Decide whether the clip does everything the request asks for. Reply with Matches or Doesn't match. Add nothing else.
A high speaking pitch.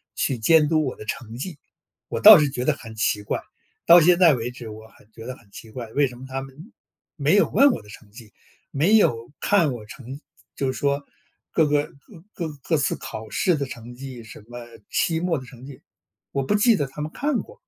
Doesn't match